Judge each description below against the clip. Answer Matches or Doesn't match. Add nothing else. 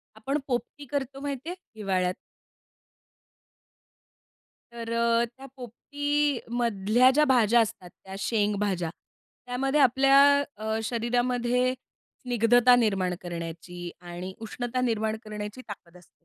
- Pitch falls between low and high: Doesn't match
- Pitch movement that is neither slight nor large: Matches